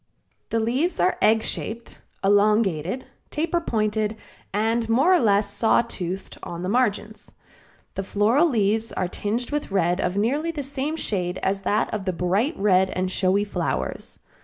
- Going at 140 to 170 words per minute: Yes, average, 160 wpm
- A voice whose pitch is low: No, high, 210 Hz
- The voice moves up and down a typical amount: Yes, average, 3.8 semitones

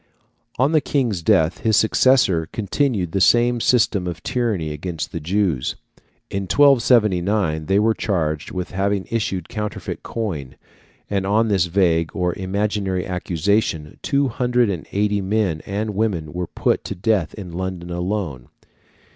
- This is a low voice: Yes, very low, 95 Hz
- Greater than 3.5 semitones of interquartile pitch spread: Yes, average, 4.0 semitones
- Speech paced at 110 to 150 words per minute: Yes, average, 145 wpm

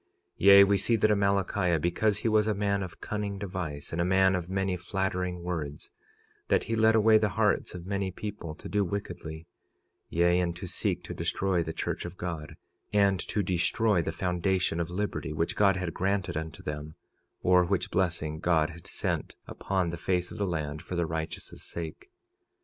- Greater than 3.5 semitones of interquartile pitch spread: No, average, 2.8 semitones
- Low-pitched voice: Yes, very low, 90 Hz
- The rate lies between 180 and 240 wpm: Yes, average, 190 wpm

